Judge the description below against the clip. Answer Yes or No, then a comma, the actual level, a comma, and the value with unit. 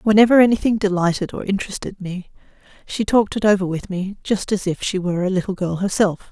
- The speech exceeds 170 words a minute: Yes, average, 200 wpm